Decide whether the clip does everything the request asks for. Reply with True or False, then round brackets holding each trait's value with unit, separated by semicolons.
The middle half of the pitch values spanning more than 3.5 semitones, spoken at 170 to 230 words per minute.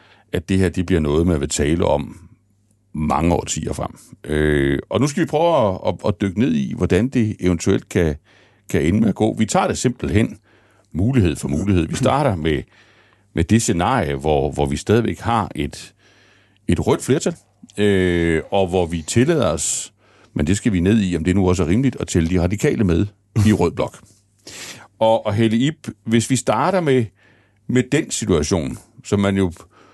True (3.9 semitones; 190 wpm)